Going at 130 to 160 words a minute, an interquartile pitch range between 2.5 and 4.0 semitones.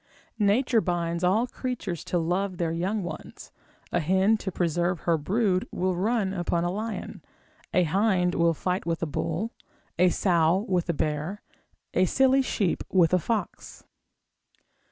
Yes: average, 155 wpm; average, 3.2 semitones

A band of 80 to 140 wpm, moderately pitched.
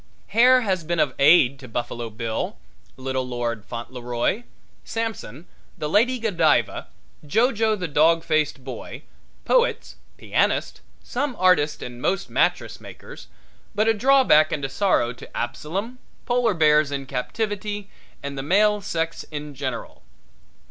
Yes: slow, 135 wpm; medium, 155 Hz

